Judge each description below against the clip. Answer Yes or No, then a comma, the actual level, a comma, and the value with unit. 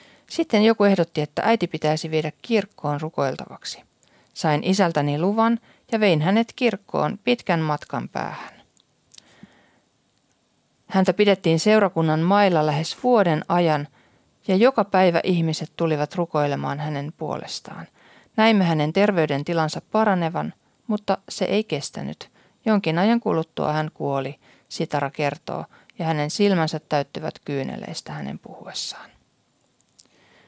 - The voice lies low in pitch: No, medium, 170 Hz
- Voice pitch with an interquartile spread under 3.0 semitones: No, average, 5.0 semitones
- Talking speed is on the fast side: No, average, 110 wpm